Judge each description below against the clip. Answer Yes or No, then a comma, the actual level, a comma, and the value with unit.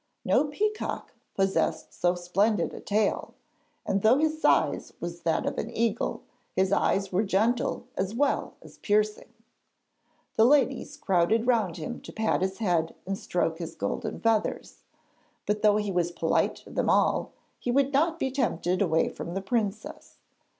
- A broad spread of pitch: No, average, 4.4 semitones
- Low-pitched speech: No, high, 210 Hz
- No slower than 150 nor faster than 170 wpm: Yes, average, 160 wpm